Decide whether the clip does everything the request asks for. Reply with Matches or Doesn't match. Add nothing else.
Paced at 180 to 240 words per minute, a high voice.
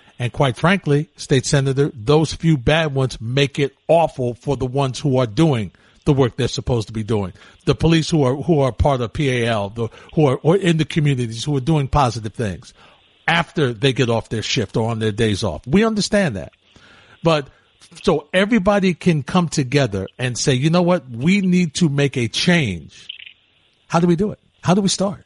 Doesn't match